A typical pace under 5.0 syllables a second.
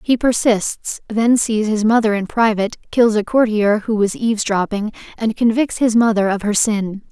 Yes: 4.8 syllables/s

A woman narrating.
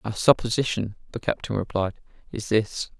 No: male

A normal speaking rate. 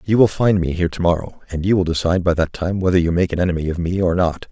No: fast, 290 wpm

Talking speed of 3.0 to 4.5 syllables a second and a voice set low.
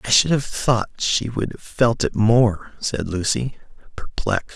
Yes: 4.2 syllables/s; low, 115 Hz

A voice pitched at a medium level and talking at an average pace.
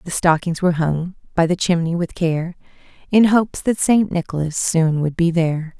Yes: medium, 170 Hz; average, 185 wpm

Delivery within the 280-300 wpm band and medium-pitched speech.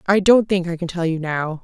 Yes: fast, 295 wpm; medium, 175 Hz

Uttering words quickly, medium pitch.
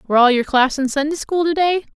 No: fast, 245 wpm; very high, 290 Hz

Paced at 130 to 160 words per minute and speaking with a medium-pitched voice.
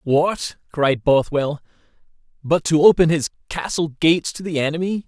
Yes: average, 140 wpm; medium, 160 Hz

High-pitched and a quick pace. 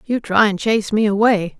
Yes: high, 210 Hz; fast, 225 wpm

